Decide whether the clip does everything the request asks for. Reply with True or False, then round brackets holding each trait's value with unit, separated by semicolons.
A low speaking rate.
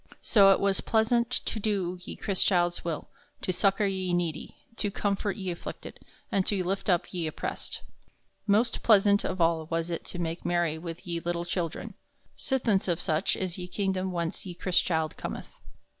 False (175 wpm)